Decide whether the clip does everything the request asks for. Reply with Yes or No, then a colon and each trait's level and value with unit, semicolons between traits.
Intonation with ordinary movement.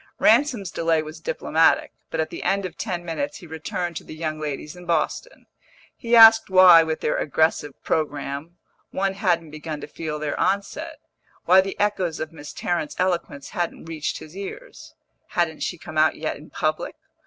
Yes: average, 3.5 semitones